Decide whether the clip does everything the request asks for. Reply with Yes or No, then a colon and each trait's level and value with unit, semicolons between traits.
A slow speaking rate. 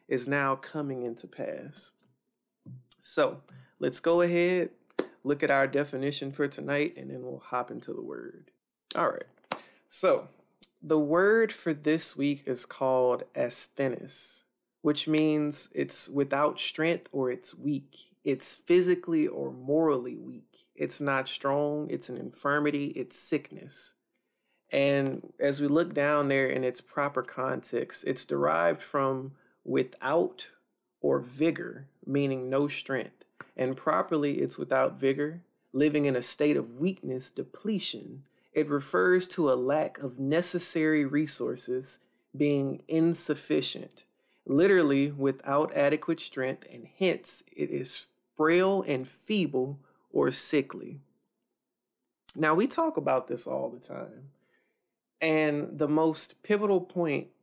Yes: slow, 125 wpm